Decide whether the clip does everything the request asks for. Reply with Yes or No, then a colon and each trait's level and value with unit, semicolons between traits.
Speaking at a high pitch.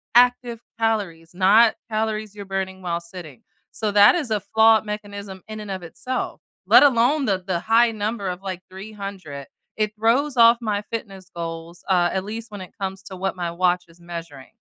Yes: high, 200 Hz